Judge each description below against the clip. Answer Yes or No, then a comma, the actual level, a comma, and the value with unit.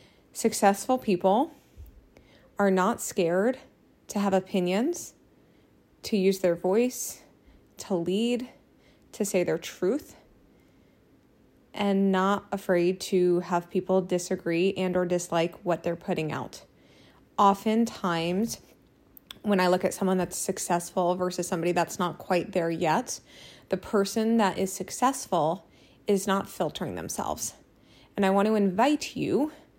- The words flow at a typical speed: No, slow, 125 wpm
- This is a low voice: No, high, 190 Hz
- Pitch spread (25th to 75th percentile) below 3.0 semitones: Yes, narrow, 2.5 semitones